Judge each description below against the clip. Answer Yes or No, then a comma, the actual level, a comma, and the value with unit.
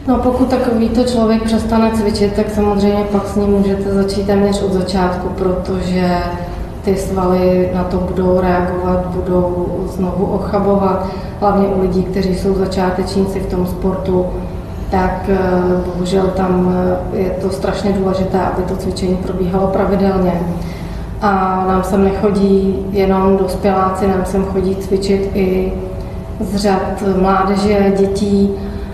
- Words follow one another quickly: No, average, 130 wpm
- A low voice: No, high, 190 Hz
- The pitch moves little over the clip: Yes, narrow, 1.3 semitones